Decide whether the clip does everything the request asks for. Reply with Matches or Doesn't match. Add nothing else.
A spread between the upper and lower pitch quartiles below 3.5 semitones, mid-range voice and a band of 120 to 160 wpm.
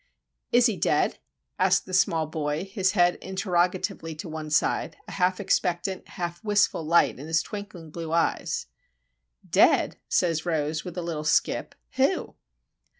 Matches